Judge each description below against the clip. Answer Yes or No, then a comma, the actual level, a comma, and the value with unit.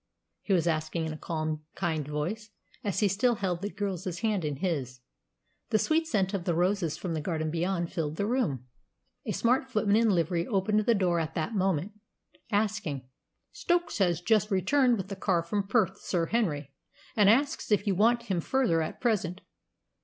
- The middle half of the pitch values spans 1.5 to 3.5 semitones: No, average, 4.5 semitones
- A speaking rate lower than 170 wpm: No, average, 185 wpm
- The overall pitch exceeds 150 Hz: Yes, high, 190 Hz